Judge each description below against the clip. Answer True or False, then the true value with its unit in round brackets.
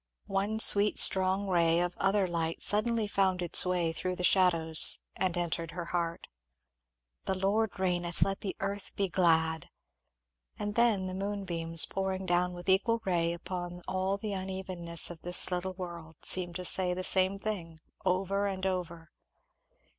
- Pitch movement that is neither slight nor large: False (2.1 semitones)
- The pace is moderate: True (155 wpm)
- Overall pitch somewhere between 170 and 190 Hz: True (185 Hz)